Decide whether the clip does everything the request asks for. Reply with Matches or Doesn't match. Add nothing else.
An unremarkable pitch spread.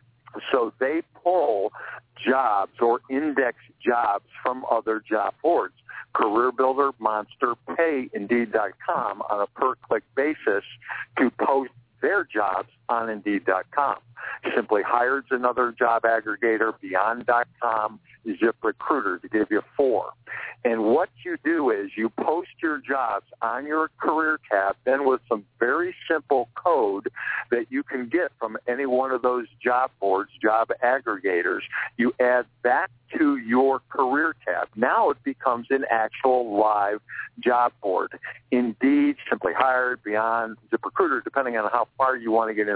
Matches